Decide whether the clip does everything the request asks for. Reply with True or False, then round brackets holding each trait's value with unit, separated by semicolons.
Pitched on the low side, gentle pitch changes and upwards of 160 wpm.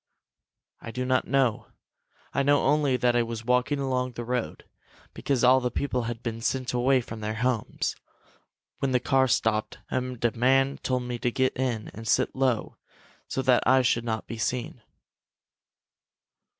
True (125 Hz; 2.0 semitones; 170 wpm)